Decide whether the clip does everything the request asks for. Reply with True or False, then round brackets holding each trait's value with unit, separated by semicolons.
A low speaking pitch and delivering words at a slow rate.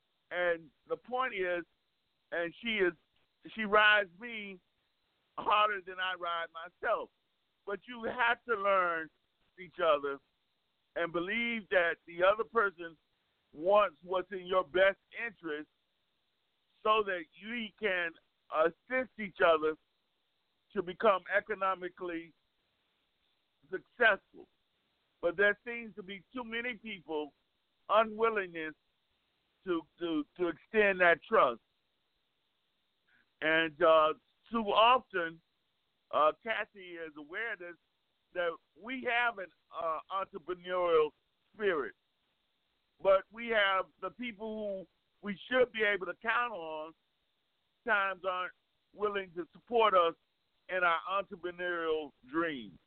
False (185 Hz; 110 wpm)